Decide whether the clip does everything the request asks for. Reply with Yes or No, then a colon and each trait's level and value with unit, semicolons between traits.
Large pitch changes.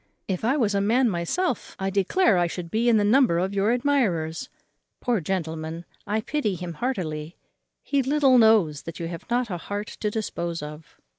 Yes: wide, 5.9 semitones